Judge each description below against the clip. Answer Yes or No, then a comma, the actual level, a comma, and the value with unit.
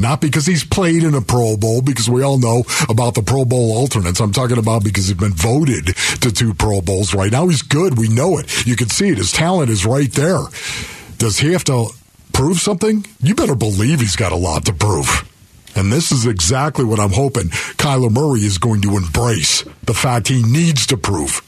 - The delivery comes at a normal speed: No, fast, 220 wpm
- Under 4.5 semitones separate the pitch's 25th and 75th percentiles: No, average, 4.9 semitones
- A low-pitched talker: Yes, low, 120 Hz